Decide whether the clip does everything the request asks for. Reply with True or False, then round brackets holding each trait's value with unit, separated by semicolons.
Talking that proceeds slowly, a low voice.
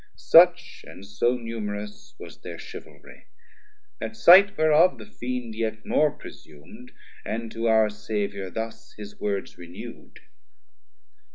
True (120 wpm; 110 Hz)